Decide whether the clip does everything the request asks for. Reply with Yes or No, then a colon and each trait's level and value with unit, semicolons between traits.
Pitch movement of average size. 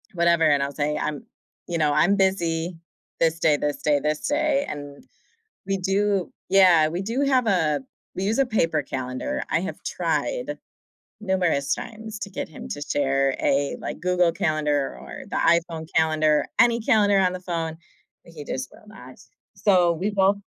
Yes: average, 4.6 semitones